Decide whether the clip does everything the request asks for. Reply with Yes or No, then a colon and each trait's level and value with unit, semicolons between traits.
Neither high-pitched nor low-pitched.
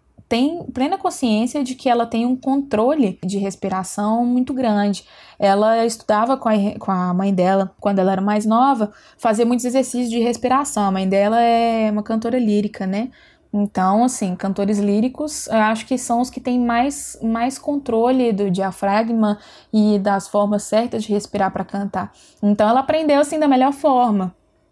No: high, 225 Hz